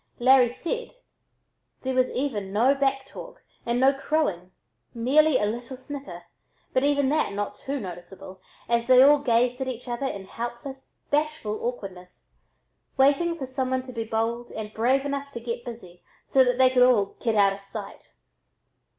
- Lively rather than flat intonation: No, average, 3.4 semitones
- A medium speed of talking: Yes, average, 165 wpm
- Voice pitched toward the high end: Yes, very high, 250 Hz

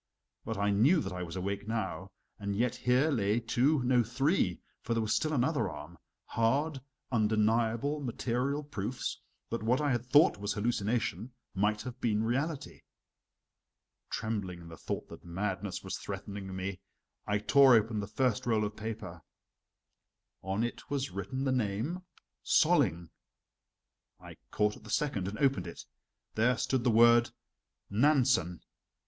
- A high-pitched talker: No, low, 110 Hz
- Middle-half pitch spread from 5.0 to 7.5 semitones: No, average, 4.1 semitones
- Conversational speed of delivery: Yes, average, 150 wpm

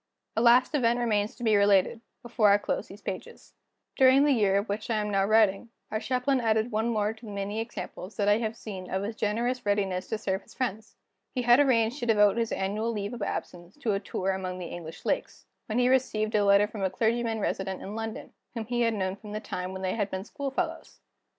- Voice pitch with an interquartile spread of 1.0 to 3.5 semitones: Yes, average, 2.9 semitones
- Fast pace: Yes, fast, 235 wpm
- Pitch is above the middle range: Yes, high, 215 Hz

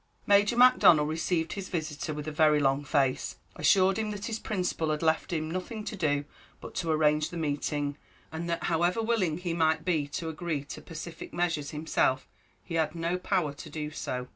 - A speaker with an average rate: Yes, average, 190 wpm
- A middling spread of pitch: Yes, average, 3.1 semitones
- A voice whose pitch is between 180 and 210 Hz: No, medium, 160 Hz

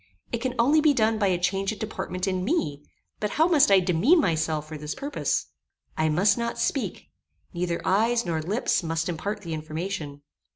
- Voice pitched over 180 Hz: Yes, high, 190 Hz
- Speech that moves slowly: No, average, 190 wpm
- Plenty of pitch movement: Yes, wide, 6.3 semitones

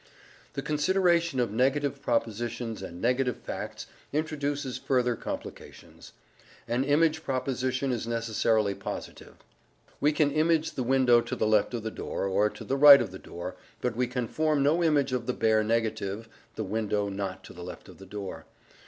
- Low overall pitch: Yes, low, 125 Hz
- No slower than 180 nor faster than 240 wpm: No, average, 170 wpm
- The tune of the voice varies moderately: Yes, average, 4.5 semitones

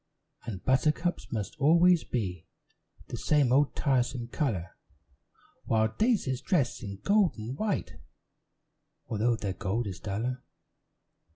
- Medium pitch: No, low, 120 Hz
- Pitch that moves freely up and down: Yes, wide, 6.1 semitones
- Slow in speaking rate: Yes, slow, 115 wpm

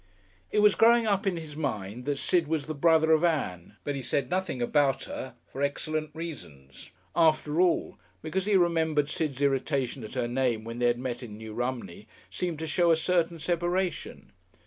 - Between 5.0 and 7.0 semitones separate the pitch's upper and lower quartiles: Yes, average, 5.3 semitones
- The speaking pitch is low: No, medium, 150 Hz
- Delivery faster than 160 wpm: Yes, average, 190 wpm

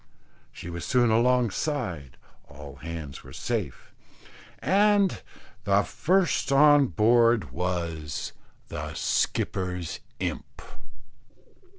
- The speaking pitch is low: Yes, low, 100 Hz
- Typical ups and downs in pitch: No, wide, 8.6 semitones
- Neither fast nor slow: No, slow, 85 wpm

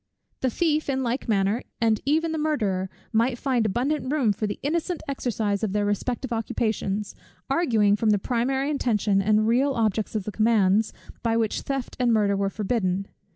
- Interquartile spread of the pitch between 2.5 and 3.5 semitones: No, average, 4.3 semitones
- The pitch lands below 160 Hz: No, high, 225 Hz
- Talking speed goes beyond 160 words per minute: Yes, average, 175 wpm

